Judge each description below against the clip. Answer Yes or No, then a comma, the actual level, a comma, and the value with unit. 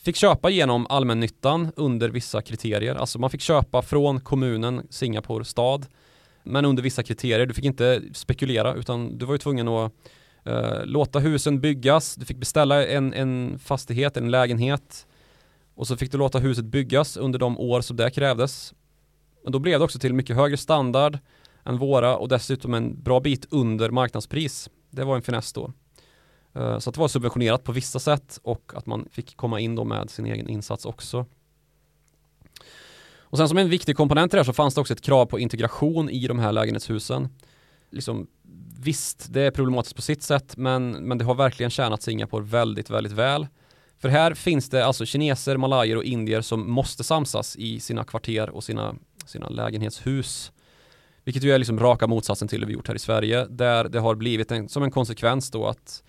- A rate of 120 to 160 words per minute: No, average, 190 wpm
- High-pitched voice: No, low, 130 Hz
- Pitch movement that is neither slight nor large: Yes, average, 3.0 semitones